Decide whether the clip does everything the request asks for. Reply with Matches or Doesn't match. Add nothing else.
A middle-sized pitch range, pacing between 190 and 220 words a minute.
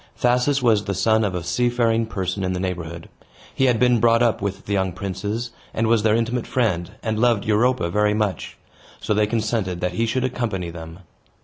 Matches